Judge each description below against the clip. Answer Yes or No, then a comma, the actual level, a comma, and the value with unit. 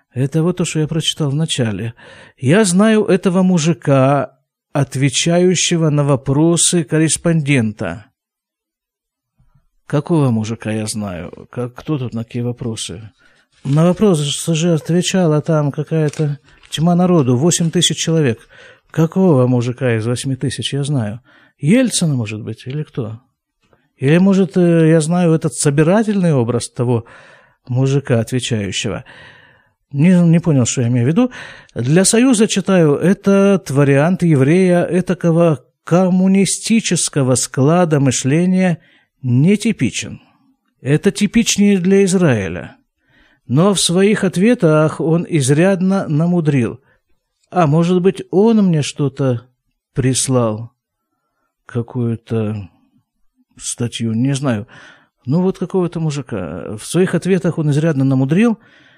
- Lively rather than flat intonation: Yes, wide, 5.8 semitones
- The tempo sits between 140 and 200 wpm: No, slow, 110 wpm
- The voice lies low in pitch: No, medium, 155 Hz